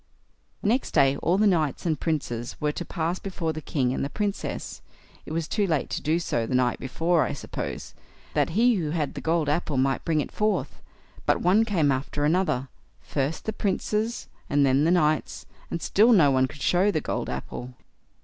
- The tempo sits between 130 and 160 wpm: No, average, 190 wpm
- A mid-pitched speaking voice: Yes, medium, 160 Hz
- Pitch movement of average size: Yes, average, 4.9 semitones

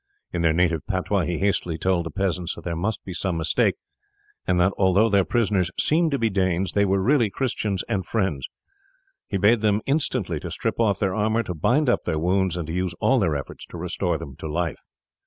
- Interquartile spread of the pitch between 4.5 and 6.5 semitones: No, average, 3.5 semitones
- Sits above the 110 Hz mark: No, very low, 95 Hz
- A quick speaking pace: Yes, fast, 220 wpm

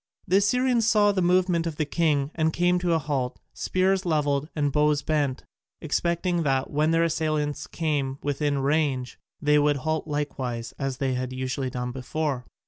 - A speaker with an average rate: Yes, average, 170 wpm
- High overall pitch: No, medium, 150 Hz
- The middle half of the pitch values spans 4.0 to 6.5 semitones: No, average, 3.5 semitones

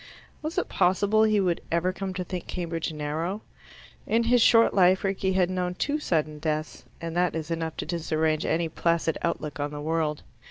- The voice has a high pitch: No, medium, 170 Hz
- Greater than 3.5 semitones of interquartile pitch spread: No, average, 3.1 semitones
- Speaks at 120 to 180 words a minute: No, average, 190 wpm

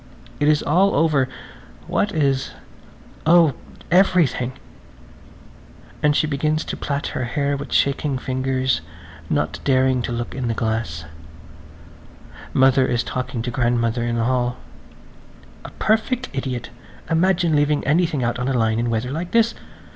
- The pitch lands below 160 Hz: Yes, low, 135 Hz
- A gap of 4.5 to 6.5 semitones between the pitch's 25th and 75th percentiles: No, average, 4.0 semitones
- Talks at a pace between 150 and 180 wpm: No, average, 140 wpm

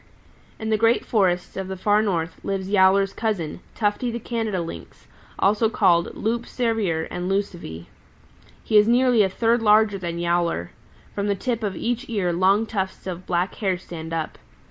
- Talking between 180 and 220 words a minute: No, average, 170 wpm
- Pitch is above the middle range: Yes, high, 195 Hz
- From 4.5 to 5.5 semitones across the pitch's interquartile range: No, average, 3.8 semitones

